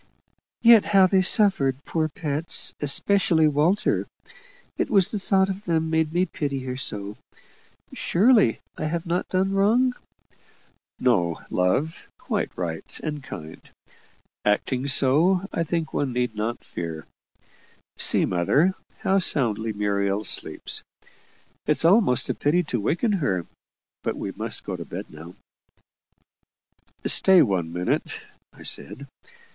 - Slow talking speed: Yes, slow, 130 wpm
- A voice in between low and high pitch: Yes, medium, 150 Hz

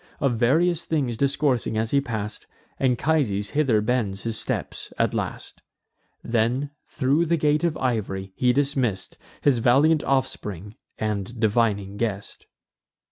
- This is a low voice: Yes, low, 120 Hz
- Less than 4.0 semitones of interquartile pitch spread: No, average, 4.8 semitones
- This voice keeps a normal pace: No, slow, 130 wpm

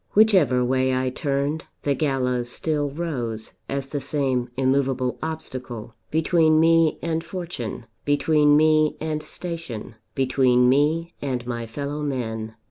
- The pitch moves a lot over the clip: No, average, 3.7 semitones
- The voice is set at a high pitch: No, medium, 140 Hz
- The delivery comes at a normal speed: No, slow, 125 wpm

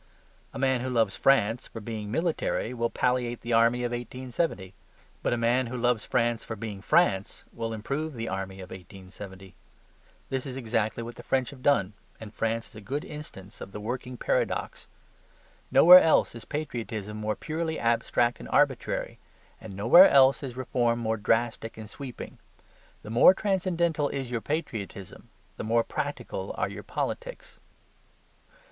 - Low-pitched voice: Yes, low, 120 Hz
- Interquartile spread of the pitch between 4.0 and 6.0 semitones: No, average, 3.5 semitones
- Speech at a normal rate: Yes, average, 160 wpm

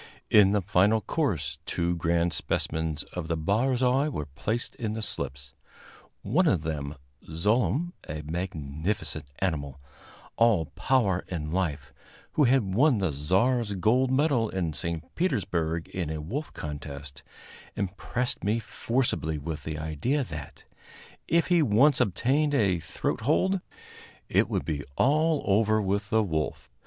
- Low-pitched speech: Yes, very low, 95 Hz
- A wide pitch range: Yes, wide, 7.7 semitones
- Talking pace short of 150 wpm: Yes, average, 140 wpm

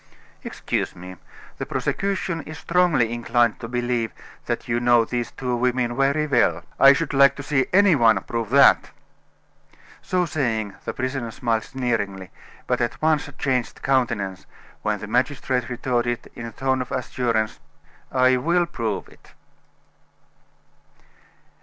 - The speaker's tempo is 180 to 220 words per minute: No, average, 140 wpm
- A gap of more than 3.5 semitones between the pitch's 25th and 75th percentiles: No, average, 3.1 semitones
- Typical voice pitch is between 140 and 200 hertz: No, low, 125 Hz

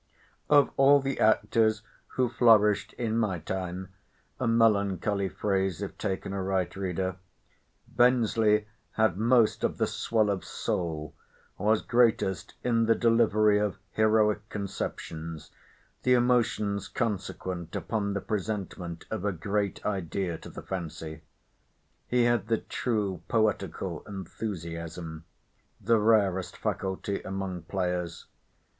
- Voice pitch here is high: No, low, 100 Hz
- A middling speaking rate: No, slow, 110 wpm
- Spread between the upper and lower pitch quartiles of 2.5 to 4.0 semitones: Yes, average, 3.1 semitones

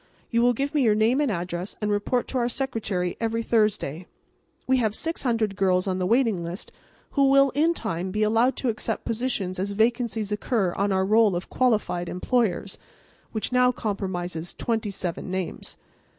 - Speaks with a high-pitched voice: Yes, high, 215 Hz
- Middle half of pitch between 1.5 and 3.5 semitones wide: No, average, 4.6 semitones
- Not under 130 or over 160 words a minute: No, average, 175 wpm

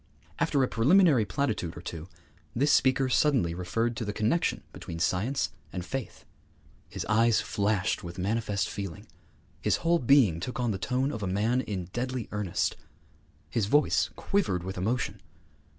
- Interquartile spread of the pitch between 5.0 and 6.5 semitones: Yes, wide, 5.4 semitones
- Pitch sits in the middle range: No, low, 110 Hz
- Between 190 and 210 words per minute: No, average, 155 wpm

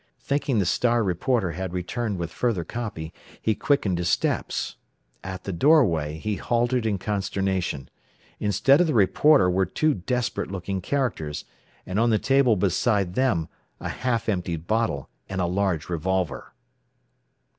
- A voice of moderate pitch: No, low, 100 Hz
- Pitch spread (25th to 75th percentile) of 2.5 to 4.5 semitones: No, average, 5.1 semitones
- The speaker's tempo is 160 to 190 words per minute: No, average, 145 wpm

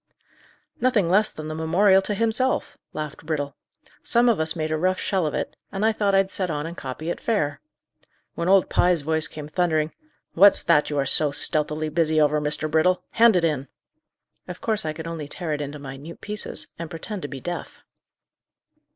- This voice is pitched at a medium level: Yes, medium, 160 Hz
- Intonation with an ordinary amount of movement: Yes, average, 4.0 semitones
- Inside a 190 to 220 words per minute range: Yes, average, 195 wpm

